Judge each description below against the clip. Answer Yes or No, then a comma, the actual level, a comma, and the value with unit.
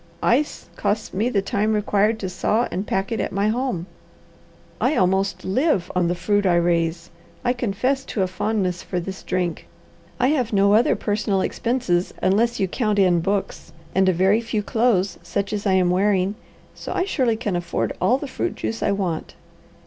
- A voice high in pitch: Yes, high, 200 Hz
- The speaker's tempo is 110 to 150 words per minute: No, average, 185 wpm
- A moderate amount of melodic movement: Yes, average, 3.6 semitones